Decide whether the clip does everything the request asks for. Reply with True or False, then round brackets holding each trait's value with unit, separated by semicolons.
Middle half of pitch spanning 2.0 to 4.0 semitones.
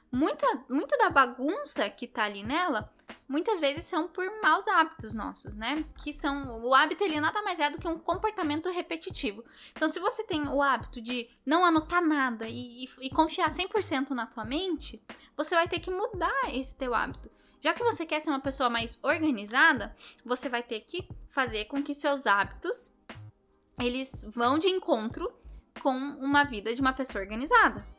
False (4.6 semitones)